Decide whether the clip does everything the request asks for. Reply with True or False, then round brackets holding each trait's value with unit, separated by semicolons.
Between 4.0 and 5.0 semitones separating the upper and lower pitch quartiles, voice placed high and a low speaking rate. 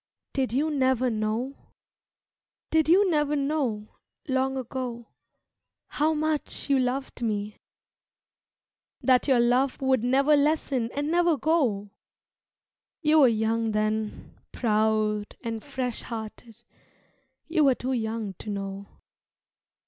True (4.6 semitones; 255 Hz; 115 wpm)